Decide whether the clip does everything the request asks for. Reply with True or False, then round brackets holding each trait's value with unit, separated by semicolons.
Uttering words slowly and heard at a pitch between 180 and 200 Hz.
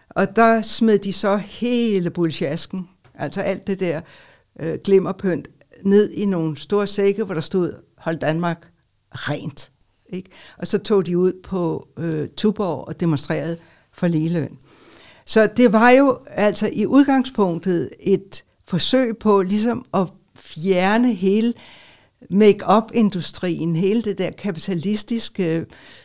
True (130 wpm; 190 Hz)